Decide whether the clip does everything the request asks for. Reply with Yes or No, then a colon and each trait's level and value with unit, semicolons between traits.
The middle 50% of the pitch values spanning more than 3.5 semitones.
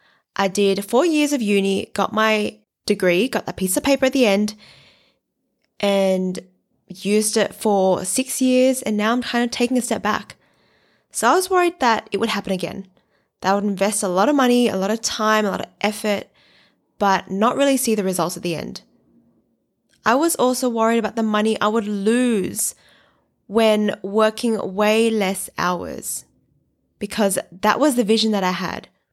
No: average, 3.2 semitones